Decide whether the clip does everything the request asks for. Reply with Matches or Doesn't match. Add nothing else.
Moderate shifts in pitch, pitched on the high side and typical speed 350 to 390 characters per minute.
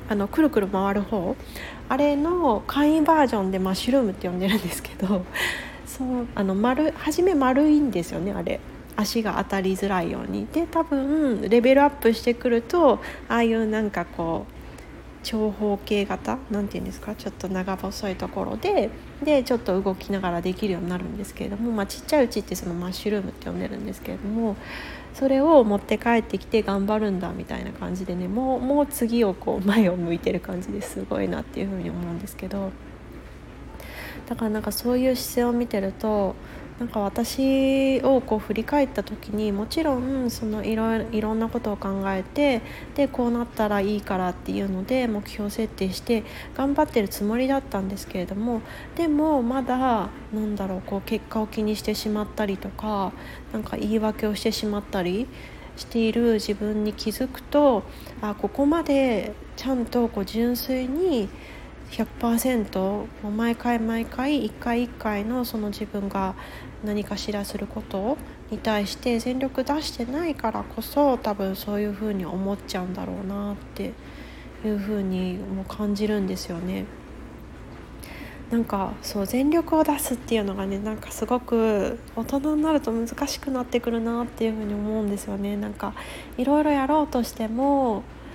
Matches